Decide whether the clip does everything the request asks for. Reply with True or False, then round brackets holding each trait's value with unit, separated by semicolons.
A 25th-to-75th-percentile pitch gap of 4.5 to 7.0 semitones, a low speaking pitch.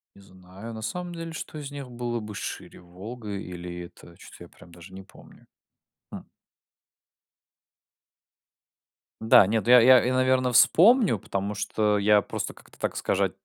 True (4.9 semitones; 110 Hz)